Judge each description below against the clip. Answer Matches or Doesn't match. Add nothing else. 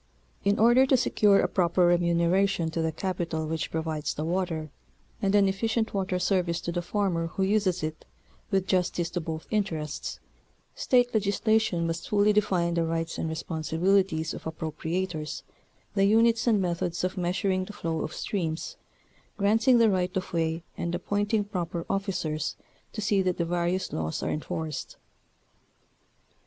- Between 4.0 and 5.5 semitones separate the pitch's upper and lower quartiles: Doesn't match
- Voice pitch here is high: Doesn't match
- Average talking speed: Matches